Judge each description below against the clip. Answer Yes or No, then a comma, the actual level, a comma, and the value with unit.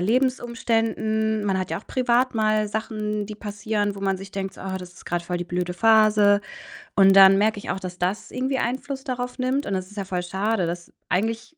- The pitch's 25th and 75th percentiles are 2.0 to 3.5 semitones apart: Yes, average, 2.8 semitones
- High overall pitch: Yes, high, 210 Hz